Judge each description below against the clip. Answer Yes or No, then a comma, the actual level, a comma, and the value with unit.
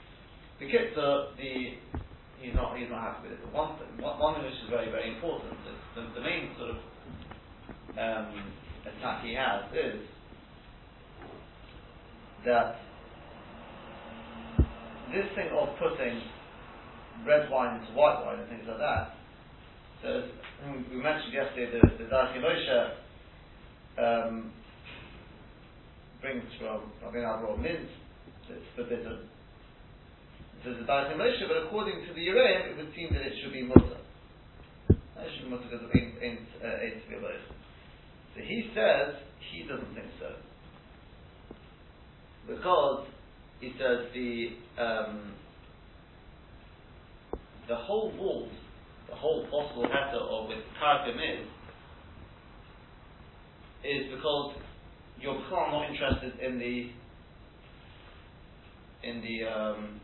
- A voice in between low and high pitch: No, low, 120 Hz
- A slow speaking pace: Yes, slow, 115 wpm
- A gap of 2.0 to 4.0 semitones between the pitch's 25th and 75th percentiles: No, average, 4.7 semitones